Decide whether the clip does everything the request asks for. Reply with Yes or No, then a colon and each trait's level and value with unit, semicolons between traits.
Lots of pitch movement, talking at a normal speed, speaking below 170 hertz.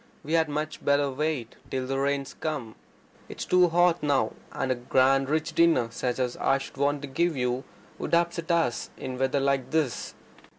No: average, 3.3 semitones; average, 185 wpm; medium, 140 Hz